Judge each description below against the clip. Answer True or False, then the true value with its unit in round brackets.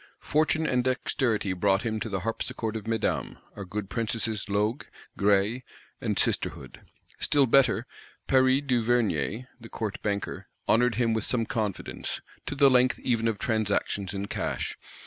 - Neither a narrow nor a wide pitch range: True (3.4 semitones)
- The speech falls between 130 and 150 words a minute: True (145 wpm)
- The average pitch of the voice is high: False (115 Hz)